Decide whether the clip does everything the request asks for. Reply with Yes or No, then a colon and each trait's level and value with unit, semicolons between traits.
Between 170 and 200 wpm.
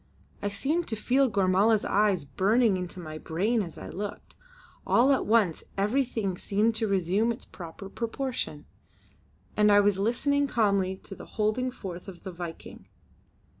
No: average, 155 wpm